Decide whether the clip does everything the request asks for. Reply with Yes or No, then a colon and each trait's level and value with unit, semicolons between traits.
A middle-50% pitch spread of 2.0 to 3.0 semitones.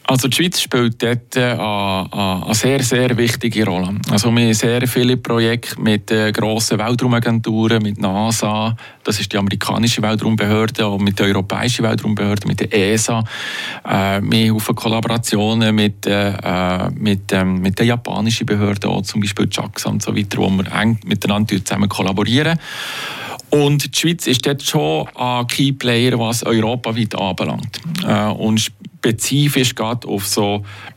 Yes: narrow, 2.6 semitones